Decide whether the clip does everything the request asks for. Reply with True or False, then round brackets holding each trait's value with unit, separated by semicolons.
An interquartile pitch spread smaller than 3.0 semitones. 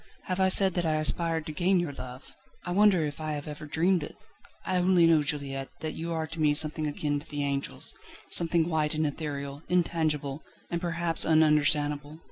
True (2.5 semitones)